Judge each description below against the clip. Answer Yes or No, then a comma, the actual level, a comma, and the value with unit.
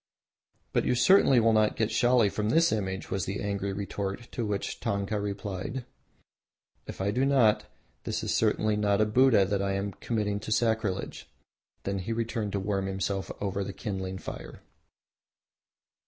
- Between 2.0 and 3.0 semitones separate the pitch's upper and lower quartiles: Yes, narrow, 2.4 semitones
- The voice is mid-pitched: No, low, 105 Hz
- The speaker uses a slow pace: No, average, 165 wpm